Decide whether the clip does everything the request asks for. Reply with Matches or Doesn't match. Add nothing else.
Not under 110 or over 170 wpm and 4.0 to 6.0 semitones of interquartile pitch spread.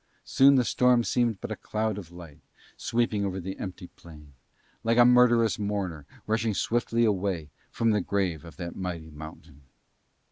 Matches